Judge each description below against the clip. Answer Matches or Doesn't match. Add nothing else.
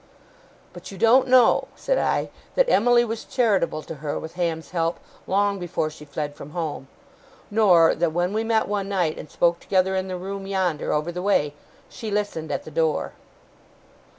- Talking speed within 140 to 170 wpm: Doesn't match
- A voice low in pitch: Doesn't match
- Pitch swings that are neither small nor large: Matches